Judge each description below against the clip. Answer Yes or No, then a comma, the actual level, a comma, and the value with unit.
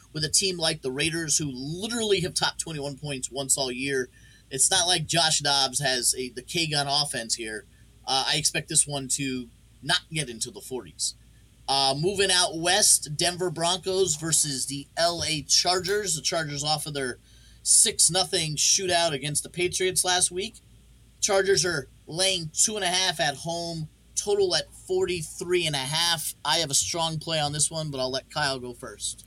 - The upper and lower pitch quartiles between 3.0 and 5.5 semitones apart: Yes, average, 4.8 semitones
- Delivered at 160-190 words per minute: Yes, average, 185 wpm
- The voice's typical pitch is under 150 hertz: No, medium, 155 Hz